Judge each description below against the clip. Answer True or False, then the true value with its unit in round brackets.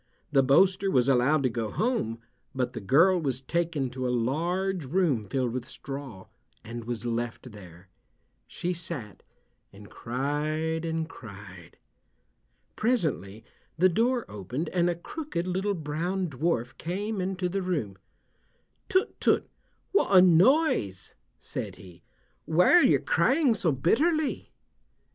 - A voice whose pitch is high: False (155 Hz)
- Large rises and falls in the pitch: True (7.4 semitones)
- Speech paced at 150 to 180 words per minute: False (135 wpm)